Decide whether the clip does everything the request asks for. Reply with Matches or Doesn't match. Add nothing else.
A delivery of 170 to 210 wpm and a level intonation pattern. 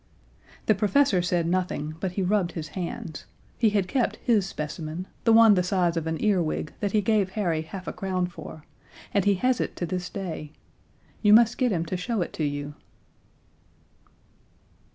Doesn't match